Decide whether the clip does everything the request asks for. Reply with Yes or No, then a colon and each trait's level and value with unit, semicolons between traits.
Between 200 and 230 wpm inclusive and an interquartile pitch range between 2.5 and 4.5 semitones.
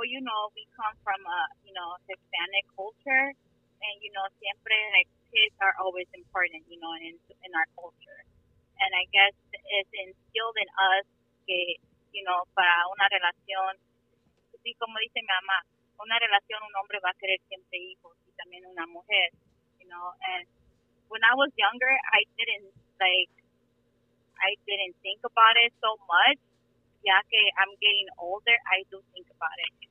No: average, 165 wpm; average, 3.1 semitones